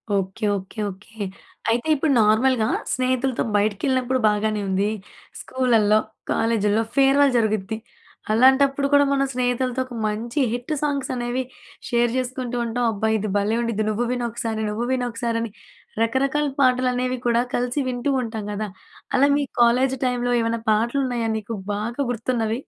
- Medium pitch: No, high, 240 Hz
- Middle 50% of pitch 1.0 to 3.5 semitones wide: Yes, average, 2.8 semitones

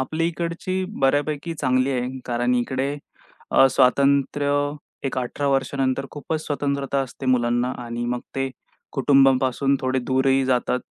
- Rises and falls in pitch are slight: Yes, narrow, 1.8 semitones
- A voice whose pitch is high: No, low, 135 Hz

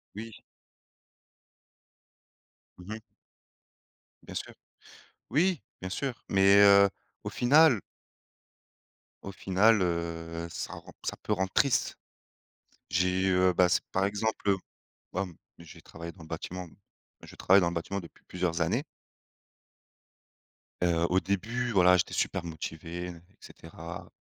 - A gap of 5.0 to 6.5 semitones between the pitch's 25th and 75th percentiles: No, average, 3.1 semitones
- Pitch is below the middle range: Yes, very low, 95 Hz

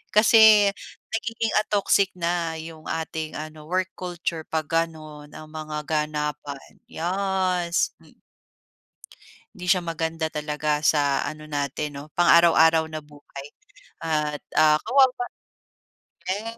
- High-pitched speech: No, medium, 160 Hz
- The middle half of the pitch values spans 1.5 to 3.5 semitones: Yes, average, 3.1 semitones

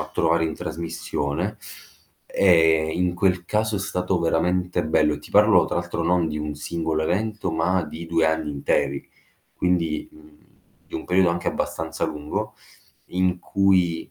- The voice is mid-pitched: No, very low, 85 Hz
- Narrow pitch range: Yes, narrow, 2.3 semitones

